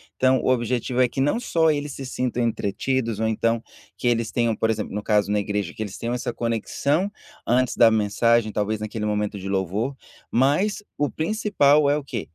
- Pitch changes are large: No, average, 4.2 semitones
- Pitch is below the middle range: Yes, low, 115 Hz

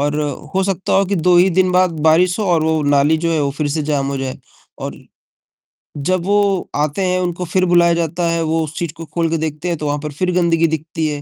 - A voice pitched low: No, medium, 165 Hz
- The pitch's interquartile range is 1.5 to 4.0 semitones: Yes, average, 2.9 semitones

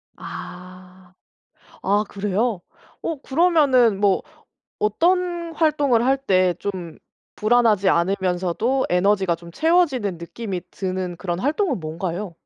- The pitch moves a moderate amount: No, wide, 5.8 semitones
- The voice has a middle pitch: No, high, 200 Hz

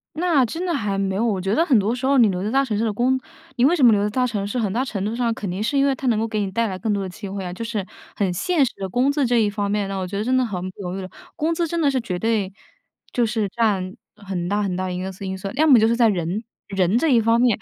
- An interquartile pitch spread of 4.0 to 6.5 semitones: Yes, average, 4.3 semitones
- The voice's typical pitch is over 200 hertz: Yes, high, 215 Hz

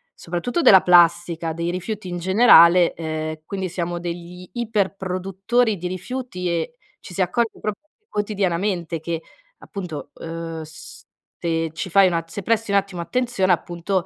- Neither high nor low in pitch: Yes, medium, 180 Hz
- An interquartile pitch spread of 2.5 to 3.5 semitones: Yes, average, 2.8 semitones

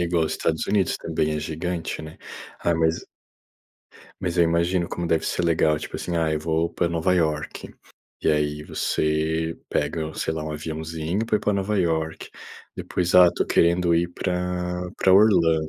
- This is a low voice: Yes, very low, 85 Hz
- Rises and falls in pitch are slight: Yes, narrow, 2.0 semitones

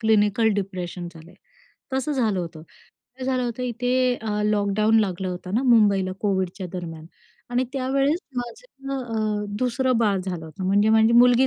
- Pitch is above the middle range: Yes, high, 220 Hz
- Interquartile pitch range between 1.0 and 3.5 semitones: No, average, 4.7 semitones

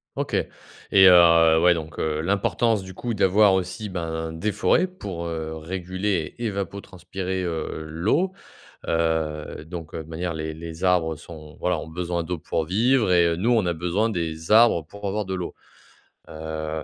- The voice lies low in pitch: Yes, very low, 85 Hz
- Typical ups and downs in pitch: Yes, average, 3.2 semitones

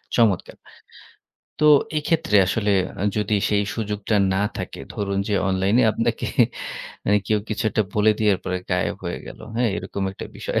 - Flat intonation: Yes, narrow, 2.0 semitones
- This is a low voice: Yes, low, 105 Hz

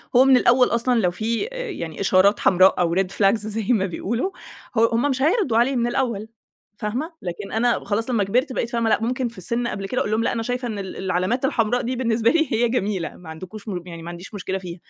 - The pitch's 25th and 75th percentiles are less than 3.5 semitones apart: No, average, 4.3 semitones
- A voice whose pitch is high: Yes, high, 225 Hz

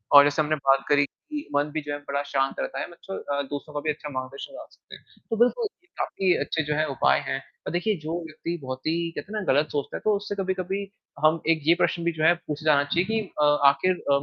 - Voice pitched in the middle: Yes, medium, 155 Hz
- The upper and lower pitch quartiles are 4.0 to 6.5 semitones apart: Yes, average, 4.3 semitones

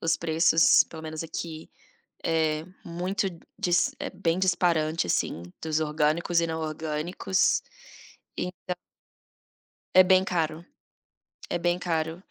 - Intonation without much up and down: Yes, narrow, 2.0 semitones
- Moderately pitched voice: Yes, medium, 165 Hz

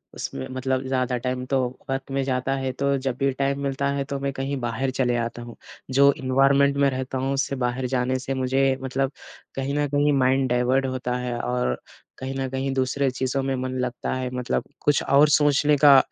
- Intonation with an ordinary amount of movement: No, narrow, 1.2 semitones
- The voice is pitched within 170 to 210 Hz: No, low, 135 Hz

